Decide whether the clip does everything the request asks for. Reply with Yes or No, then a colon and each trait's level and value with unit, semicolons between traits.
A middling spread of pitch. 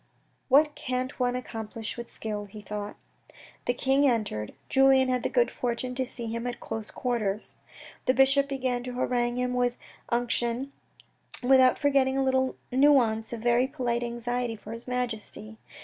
No: narrow, 2.1 semitones